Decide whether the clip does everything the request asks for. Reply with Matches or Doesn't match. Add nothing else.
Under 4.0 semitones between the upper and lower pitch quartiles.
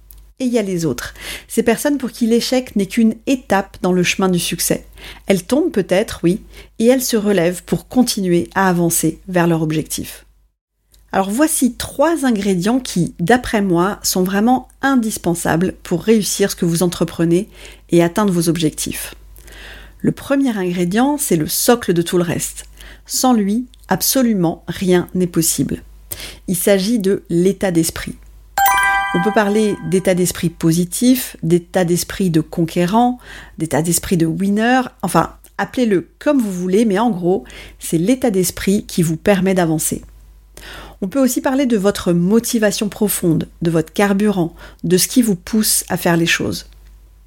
Doesn't match